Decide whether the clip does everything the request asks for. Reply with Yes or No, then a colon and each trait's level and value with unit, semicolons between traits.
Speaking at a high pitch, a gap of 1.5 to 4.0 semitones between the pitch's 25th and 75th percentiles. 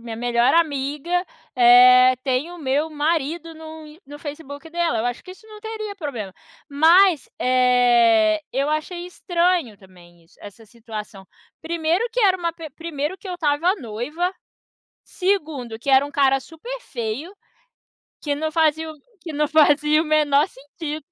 No: very high, 295 Hz; average, 5.0 semitones